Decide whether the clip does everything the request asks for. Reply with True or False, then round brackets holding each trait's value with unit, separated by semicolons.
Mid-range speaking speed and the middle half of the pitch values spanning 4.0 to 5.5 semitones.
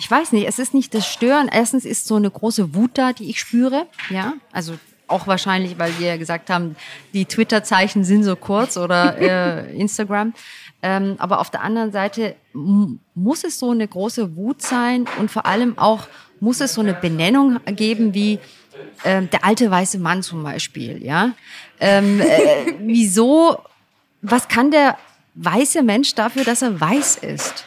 True (175 wpm; 4.4 semitones)